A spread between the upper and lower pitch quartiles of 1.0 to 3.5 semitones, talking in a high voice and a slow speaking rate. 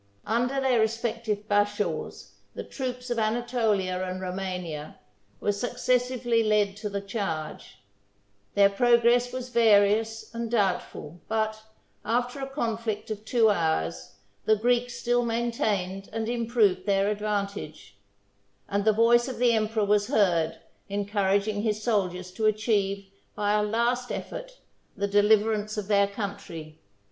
Yes: average, 2.8 semitones; high, 215 Hz; slow, 130 wpm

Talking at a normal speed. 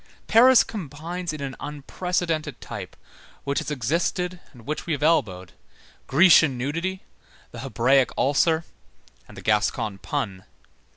No: slow, 125 wpm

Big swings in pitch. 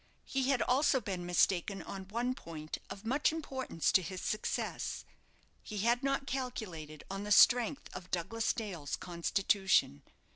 Yes: wide, 6.0 semitones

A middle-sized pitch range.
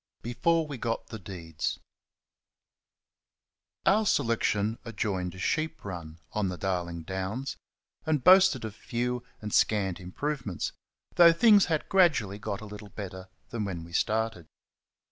No: wide, 7.2 semitones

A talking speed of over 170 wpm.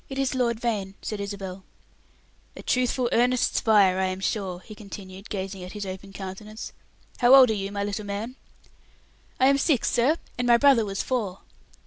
Yes: average, 180 wpm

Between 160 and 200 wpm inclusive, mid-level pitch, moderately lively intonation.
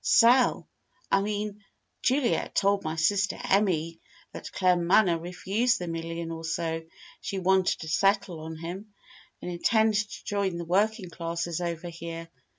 No: average, 145 wpm; medium, 180 Hz; average, 3.4 semitones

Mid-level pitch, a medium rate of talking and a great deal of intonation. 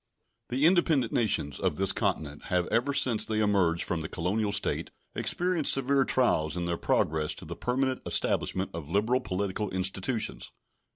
No: low, 105 Hz; average, 160 wpm; wide, 6.8 semitones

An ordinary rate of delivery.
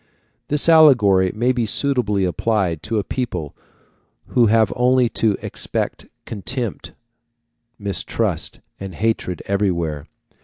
No: slow, 110 wpm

